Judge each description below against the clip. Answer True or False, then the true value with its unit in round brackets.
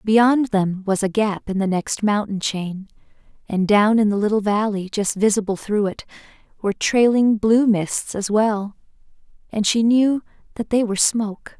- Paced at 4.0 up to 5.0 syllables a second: True (4.5 syllables/s)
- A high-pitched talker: True (210 Hz)